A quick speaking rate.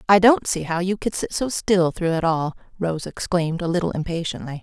Yes: fast, 220 wpm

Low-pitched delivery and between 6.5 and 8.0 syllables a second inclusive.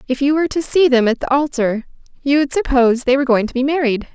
No: very high, 270 Hz; 6.7 syllables/s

